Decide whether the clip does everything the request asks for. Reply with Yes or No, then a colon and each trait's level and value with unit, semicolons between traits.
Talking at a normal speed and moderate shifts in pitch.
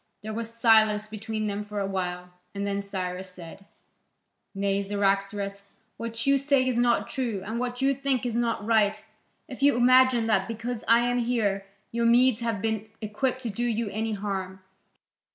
Yes: average, 175 wpm; average, 3.2 semitones